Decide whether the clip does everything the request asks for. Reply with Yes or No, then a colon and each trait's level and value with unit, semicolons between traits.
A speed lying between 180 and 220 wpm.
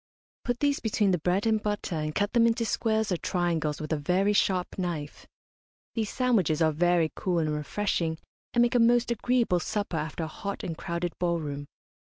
Yes: average, 190 wpm